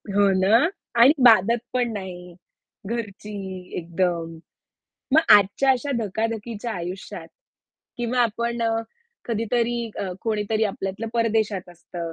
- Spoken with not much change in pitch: No, average, 3.7 semitones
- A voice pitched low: No, high, 215 Hz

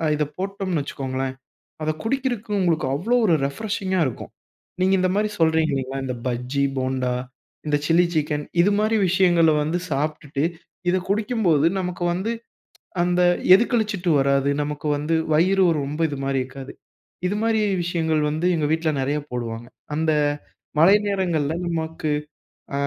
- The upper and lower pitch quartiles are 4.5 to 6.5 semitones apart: Yes, average, 5.0 semitones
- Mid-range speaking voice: Yes, medium, 160 Hz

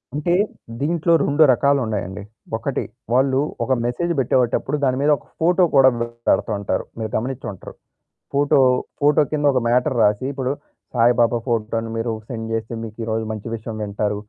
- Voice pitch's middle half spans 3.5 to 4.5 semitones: Yes, average, 3.9 semitones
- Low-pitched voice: Yes, low, 120 Hz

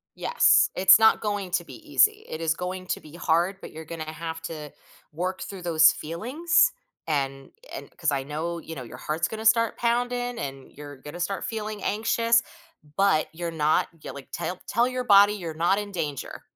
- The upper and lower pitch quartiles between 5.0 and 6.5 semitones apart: Yes, wide, 5.5 semitones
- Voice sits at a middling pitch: Yes, medium, 175 Hz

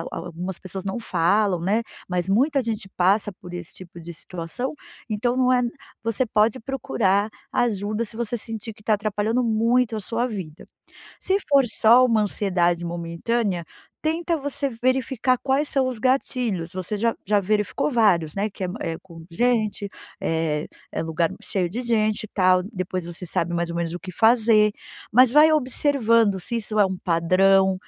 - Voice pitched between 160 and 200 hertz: No, high, 210 Hz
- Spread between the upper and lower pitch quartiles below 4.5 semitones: No, average, 4.8 semitones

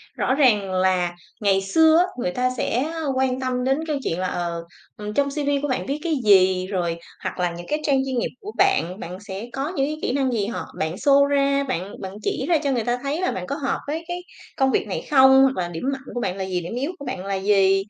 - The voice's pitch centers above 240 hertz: Yes, very high, 250 Hz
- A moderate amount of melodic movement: No, wide, 6.7 semitones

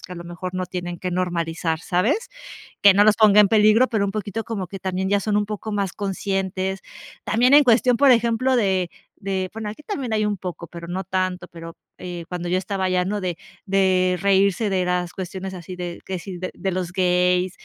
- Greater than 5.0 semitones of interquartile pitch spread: No, narrow, 2.6 semitones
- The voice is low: No, high, 190 Hz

